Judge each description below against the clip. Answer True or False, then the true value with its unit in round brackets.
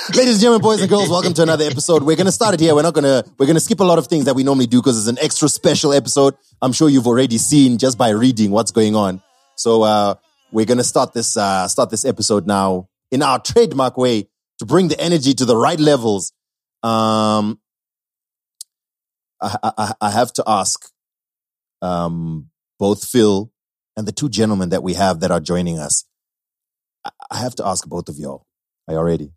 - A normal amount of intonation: False (6.5 semitones)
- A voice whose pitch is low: True (125 Hz)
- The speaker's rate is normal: False (215 wpm)